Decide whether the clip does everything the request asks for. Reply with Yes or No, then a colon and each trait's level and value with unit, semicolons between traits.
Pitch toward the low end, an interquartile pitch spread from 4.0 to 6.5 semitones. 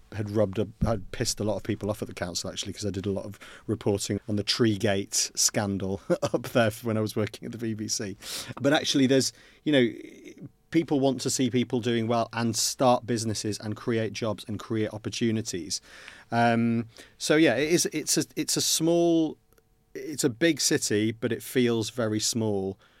No: low, 115 Hz; average, 2.9 semitones